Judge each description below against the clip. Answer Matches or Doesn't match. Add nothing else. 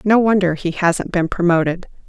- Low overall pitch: Doesn't match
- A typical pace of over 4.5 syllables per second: Matches